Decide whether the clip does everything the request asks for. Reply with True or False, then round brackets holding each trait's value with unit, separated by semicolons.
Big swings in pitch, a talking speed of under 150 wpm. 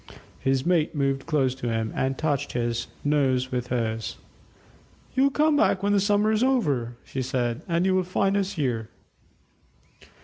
False (7.4 semitones; 165 wpm)